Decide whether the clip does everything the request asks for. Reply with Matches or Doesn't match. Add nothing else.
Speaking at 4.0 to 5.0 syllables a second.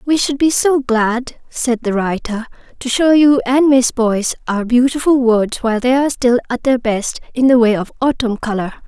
Matches